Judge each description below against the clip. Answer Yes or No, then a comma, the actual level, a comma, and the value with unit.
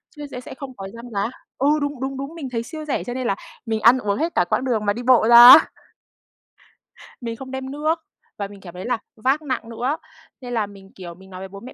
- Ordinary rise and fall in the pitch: Yes, average, 4.6 semitones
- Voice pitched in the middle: No, high, 245 Hz